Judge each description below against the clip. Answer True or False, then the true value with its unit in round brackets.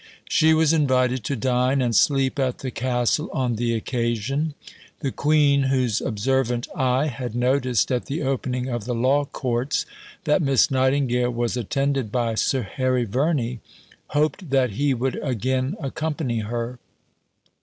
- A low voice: True (130 Hz)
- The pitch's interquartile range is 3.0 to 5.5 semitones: False (2.5 semitones)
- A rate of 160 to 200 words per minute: False (145 wpm)